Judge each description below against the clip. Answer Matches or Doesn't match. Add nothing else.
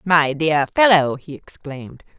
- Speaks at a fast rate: Doesn't match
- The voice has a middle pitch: Matches